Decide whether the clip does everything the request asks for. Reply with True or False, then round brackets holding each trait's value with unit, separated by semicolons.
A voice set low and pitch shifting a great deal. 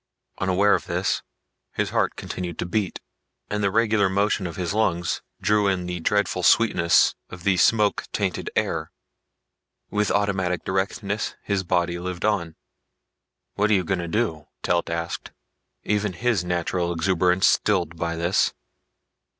False (95 Hz; 2.9 semitones)